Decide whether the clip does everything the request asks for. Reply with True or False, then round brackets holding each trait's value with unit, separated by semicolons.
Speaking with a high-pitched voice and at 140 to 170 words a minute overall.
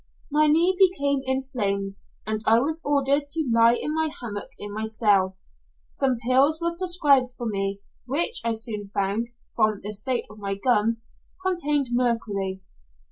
True (240 Hz; 155 wpm)